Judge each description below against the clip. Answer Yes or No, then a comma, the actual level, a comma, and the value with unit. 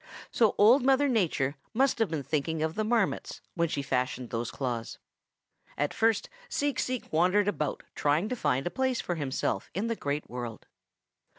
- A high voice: No, medium, 170 Hz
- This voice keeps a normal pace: Yes, average, 175 wpm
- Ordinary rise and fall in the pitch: No, wide, 8.5 semitones